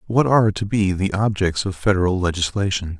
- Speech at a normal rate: Yes, average, 180 wpm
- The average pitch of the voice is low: Yes, low, 100 Hz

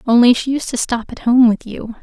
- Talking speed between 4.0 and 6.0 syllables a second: Yes, 5.4 syllables/s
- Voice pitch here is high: Yes, high, 240 Hz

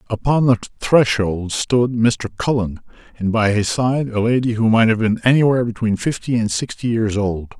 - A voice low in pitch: Yes, low, 115 Hz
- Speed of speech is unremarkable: Yes, average, 180 wpm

